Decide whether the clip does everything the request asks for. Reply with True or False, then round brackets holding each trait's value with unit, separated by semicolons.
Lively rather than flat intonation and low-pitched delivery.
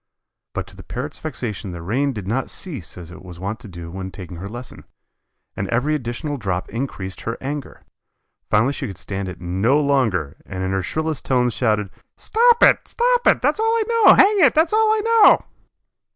True (8.4 semitones; 120 Hz)